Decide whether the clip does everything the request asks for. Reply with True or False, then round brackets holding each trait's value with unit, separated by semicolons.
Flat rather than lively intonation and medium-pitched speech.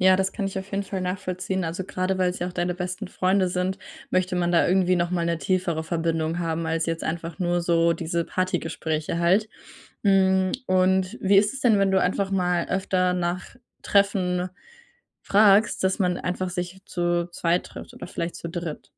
True (1.7 semitones; 180 Hz)